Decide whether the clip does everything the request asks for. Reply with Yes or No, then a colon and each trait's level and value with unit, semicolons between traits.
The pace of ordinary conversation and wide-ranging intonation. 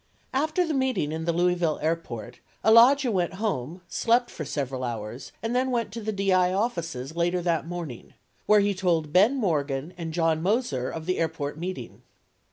Yes: average, 175 wpm; wide, 5.7 semitones